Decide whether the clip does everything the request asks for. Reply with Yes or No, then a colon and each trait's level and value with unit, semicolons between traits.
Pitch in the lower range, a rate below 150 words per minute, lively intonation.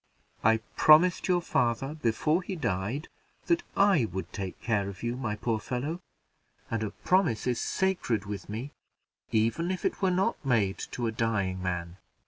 No: low, 120 Hz; average, 165 wpm; wide, 7.9 semitones